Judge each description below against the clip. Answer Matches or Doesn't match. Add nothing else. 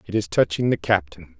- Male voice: Matches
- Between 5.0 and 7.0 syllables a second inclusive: Matches